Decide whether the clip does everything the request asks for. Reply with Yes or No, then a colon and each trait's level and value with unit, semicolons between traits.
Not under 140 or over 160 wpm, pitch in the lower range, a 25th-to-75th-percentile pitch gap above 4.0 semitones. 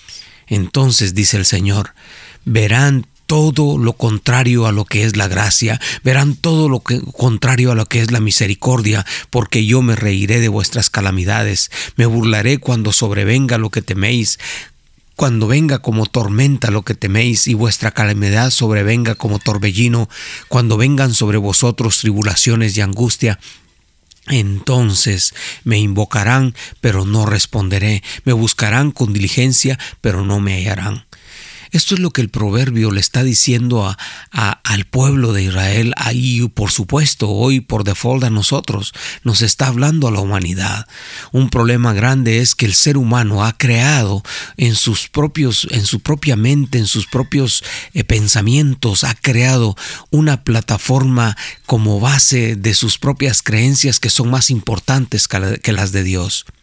No: average, 150 wpm; low, 115 Hz; average, 3.5 semitones